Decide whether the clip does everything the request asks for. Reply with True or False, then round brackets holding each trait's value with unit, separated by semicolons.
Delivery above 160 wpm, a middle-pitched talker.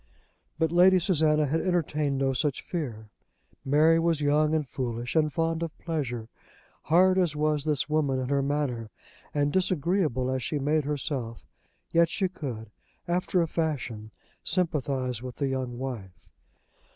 False (150 wpm; 150 Hz)